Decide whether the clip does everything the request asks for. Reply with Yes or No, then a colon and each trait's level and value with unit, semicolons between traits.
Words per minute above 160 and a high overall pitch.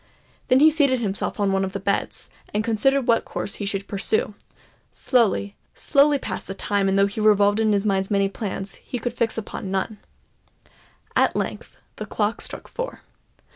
Yes: average, 175 wpm; high, 210 Hz